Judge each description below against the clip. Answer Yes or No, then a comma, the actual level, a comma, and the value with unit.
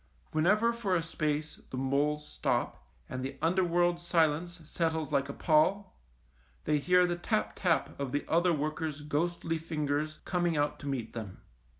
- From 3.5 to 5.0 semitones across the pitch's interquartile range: No, average, 3.0 semitones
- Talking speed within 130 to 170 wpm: Yes, average, 160 wpm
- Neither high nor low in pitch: Yes, medium, 155 Hz